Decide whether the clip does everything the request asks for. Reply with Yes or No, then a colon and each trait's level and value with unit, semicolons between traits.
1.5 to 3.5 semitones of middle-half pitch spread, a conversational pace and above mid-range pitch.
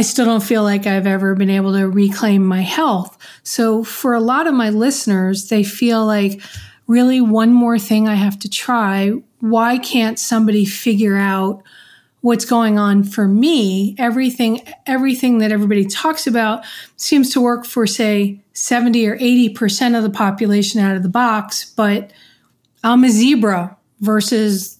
Yes: average, 3.2 semitones; average, 160 wpm; high, 220 Hz